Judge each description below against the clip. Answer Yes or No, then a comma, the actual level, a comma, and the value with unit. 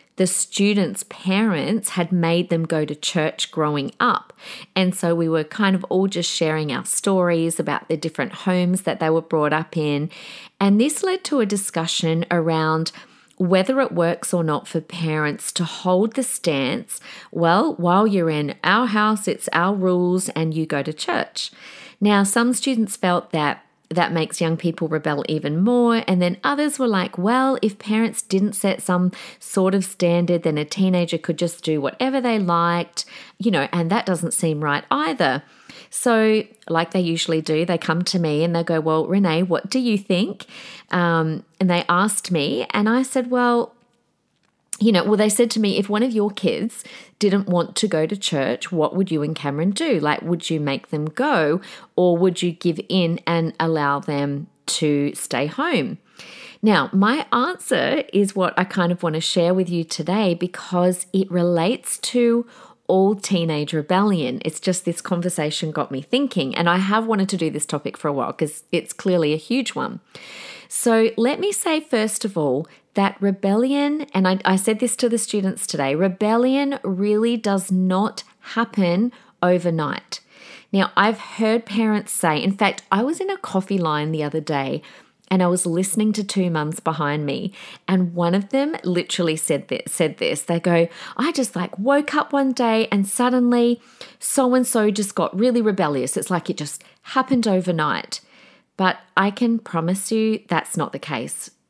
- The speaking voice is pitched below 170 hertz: No, medium, 185 Hz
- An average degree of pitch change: Yes, average, 5.0 semitones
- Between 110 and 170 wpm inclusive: No, average, 185 wpm